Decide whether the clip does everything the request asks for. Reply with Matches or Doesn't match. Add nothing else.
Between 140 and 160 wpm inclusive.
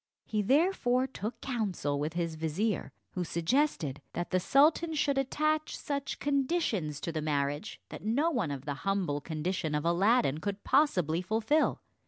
Matches